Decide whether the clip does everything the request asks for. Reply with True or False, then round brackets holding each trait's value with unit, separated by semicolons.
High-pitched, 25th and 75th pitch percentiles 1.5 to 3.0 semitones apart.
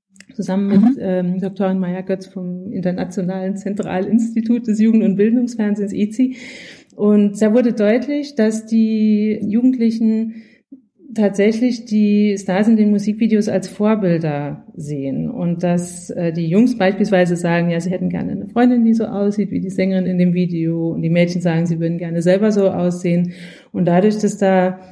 False (200 Hz; 3.4 semitones)